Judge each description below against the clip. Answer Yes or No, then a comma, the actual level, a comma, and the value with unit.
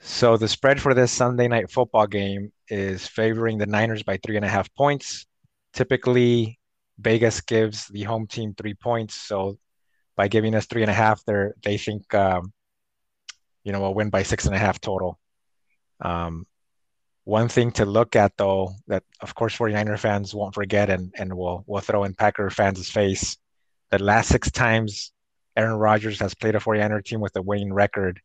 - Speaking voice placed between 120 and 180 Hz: No, low, 105 Hz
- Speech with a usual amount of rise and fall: No, narrow, 2.3 semitones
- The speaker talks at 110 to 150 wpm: No, average, 185 wpm